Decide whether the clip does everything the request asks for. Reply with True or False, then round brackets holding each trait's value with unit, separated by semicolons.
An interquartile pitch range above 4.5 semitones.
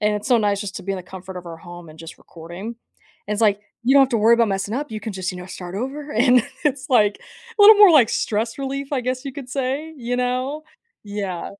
True (5.5 semitones)